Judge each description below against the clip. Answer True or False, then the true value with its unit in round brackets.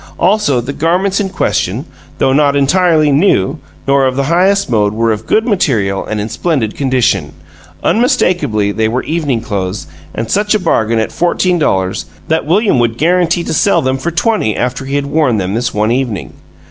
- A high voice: False (140 Hz)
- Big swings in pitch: True (7.6 semitones)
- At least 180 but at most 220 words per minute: True (185 wpm)